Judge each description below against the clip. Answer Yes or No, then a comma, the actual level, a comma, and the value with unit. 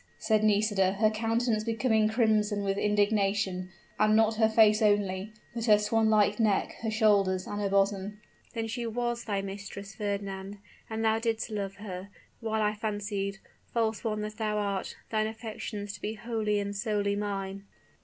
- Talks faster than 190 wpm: No, average, 165 wpm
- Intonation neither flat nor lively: No, narrow, 1.6 semitones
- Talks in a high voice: Yes, high, 210 Hz